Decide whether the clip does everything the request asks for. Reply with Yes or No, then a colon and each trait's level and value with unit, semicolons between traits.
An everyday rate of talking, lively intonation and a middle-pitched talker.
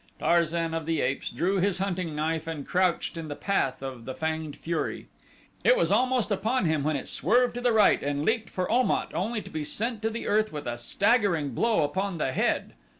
No: fast, 210 wpm; wide, 6.1 semitones; medium, 170 Hz